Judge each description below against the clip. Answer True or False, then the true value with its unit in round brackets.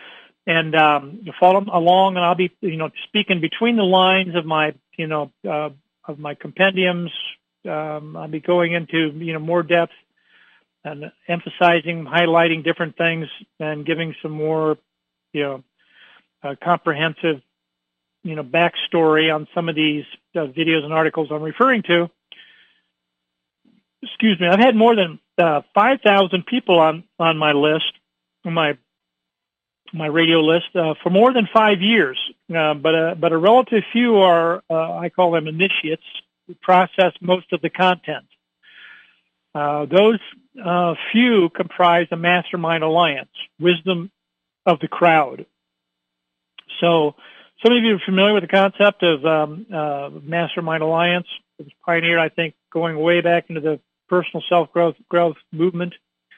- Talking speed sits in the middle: True (150 wpm)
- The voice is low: False (165 Hz)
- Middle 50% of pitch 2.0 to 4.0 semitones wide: True (2.8 semitones)